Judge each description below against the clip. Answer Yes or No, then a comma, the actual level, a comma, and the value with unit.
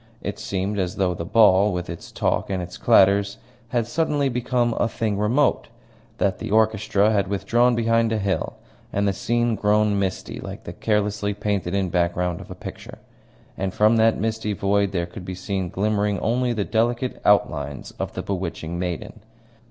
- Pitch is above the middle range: No, low, 105 Hz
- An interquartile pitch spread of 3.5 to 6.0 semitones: No, average, 3.0 semitones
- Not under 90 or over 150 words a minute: No, average, 175 wpm